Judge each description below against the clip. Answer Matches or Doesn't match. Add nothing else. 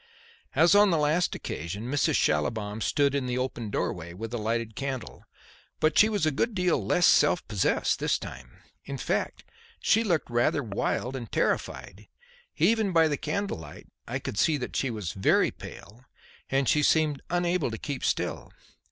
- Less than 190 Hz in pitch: Matches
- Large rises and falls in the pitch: Matches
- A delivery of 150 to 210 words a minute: Matches